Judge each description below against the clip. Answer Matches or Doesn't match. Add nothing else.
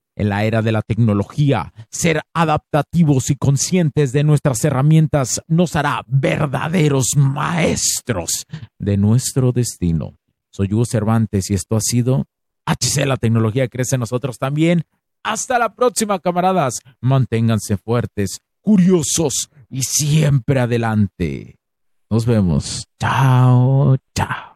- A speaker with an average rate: Doesn't match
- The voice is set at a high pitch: Doesn't match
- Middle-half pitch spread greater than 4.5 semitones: Matches